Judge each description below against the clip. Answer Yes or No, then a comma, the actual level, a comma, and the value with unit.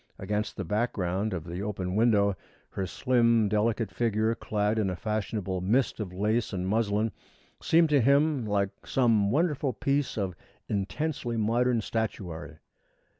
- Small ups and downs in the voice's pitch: No, average, 3.2 semitones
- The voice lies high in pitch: No, low, 110 Hz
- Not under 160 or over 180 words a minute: No, average, 140 wpm